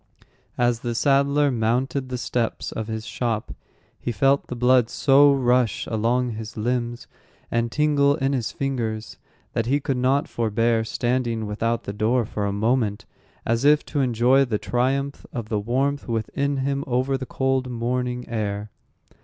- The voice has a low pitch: Yes, low, 125 Hz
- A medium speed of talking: Yes, average, 160 wpm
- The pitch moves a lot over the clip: No, average, 2.9 semitones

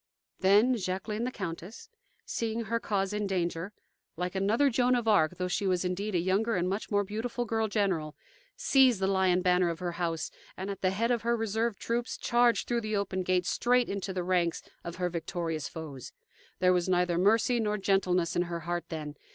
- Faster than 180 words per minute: Yes, average, 200 wpm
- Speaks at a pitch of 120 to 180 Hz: No, high, 195 Hz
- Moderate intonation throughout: Yes, average, 3.9 semitones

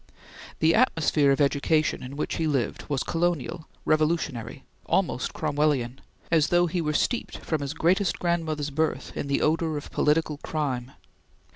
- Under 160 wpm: Yes, average, 150 wpm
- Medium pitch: Yes, medium, 155 Hz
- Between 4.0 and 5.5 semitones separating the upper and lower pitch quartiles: No, narrow, 2.6 semitones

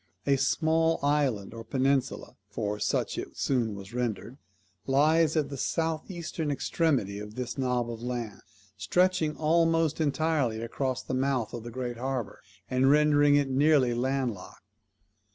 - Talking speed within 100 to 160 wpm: Yes, average, 150 wpm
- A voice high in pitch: No, low, 135 Hz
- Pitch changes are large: No, average, 4.3 semitones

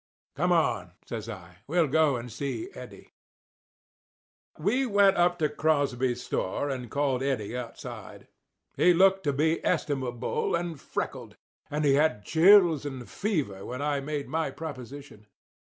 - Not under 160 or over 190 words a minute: No, average, 140 wpm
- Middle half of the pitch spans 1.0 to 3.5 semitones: No, average, 4.9 semitones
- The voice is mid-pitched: Yes, medium, 145 Hz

